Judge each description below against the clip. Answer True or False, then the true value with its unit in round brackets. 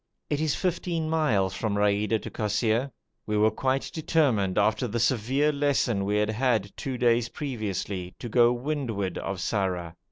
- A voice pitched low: True (115 Hz)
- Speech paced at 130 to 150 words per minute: False (165 wpm)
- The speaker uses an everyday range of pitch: True (5.0 semitones)